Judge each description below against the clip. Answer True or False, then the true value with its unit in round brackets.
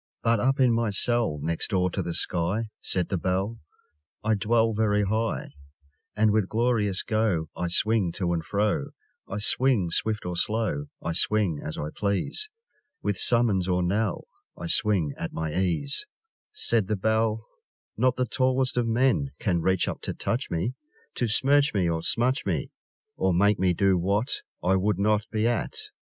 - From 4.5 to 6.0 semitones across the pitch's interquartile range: False (4.1 semitones)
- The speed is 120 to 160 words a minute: False (175 wpm)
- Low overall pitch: True (105 Hz)